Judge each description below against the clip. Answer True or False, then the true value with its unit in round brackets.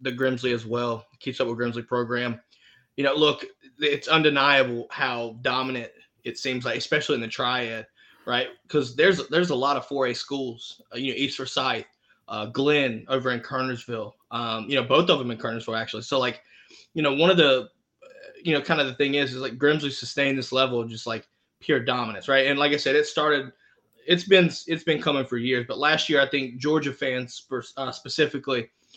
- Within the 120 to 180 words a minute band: False (205 wpm)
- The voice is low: True (130 Hz)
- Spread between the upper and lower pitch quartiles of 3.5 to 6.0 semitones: False (2.9 semitones)